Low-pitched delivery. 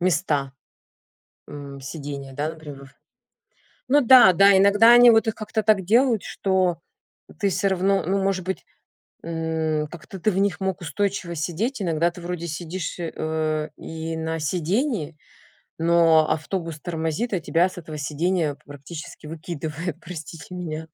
No: medium, 170 Hz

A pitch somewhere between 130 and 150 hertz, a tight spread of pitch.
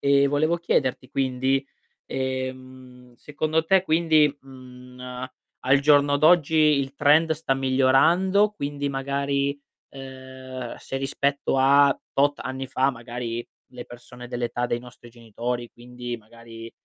Yes: low, 135 Hz; narrow, 2.3 semitones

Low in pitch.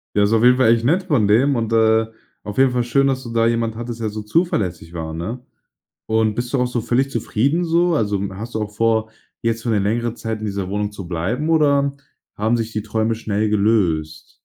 Yes: low, 115 Hz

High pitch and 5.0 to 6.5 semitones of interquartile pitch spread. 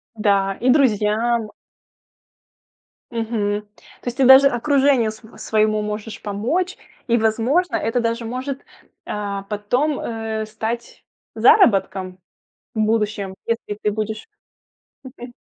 No: high, 225 Hz; average, 2.7 semitones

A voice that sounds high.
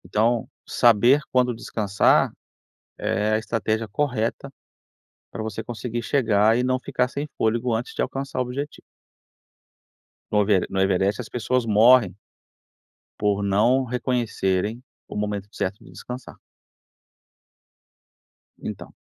No: low, 115 Hz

